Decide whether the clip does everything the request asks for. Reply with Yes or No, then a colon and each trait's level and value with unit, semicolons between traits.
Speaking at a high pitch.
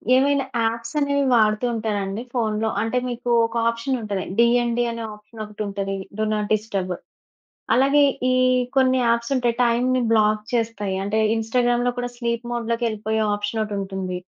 Yes: high, 230 Hz